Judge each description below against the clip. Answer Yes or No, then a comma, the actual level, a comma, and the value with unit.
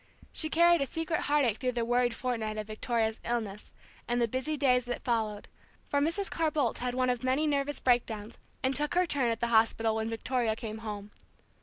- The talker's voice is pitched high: Yes, high, 245 Hz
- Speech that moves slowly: No, fast, 205 wpm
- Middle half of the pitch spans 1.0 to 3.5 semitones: No, average, 4.2 semitones